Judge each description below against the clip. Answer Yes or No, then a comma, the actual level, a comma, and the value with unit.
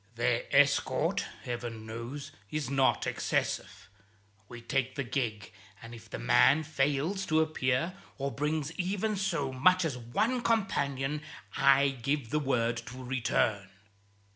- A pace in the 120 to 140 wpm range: Yes, slow, 135 wpm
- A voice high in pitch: No, low, 135 Hz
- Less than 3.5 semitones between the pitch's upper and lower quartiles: No, average, 4.2 semitones